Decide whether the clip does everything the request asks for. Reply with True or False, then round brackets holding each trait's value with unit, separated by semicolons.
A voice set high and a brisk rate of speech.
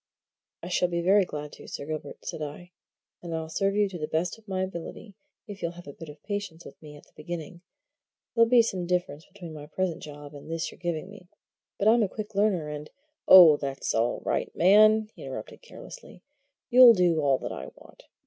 False (175 Hz; 215 wpm)